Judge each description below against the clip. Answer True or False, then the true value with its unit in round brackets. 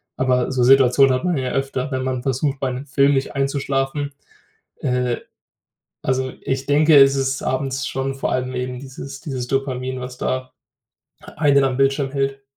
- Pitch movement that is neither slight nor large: False (1.2 semitones)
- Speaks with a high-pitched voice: False (135 Hz)